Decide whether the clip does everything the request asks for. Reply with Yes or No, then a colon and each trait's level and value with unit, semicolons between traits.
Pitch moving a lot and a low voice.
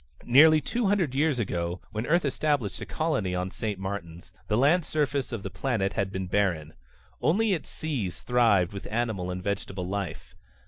Yes: wide, 7.8 semitones; low, 105 Hz